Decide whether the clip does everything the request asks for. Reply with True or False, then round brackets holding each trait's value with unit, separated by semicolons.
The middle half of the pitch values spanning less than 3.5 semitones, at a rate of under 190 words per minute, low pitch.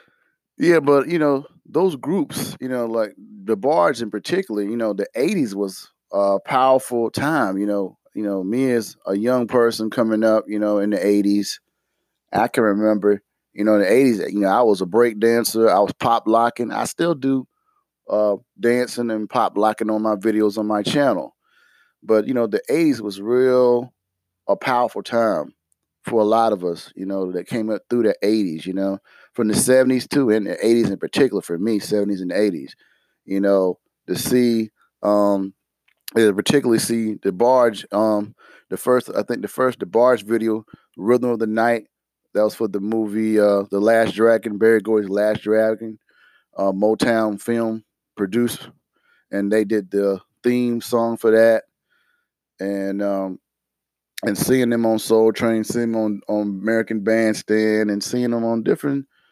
True (2.5 semitones; 175 wpm; 110 Hz)